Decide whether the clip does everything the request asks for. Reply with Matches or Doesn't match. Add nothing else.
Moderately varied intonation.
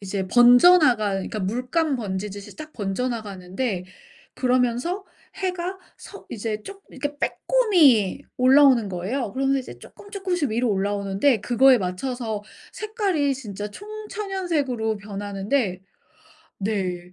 Doesn't match